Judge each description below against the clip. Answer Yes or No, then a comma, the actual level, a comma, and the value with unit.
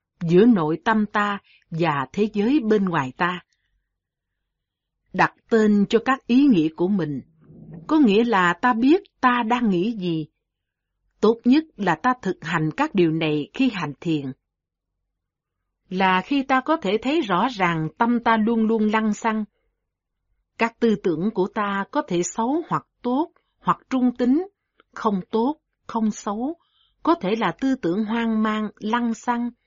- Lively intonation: Yes, wide, 5.8 semitones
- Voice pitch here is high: Yes, high, 215 Hz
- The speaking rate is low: Yes, slow, 160 wpm